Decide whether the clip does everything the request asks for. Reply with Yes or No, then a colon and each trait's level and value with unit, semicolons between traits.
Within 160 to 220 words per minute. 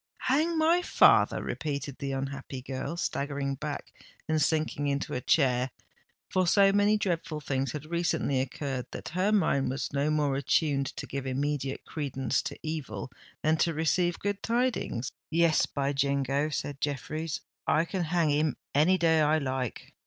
No: average, 150 wpm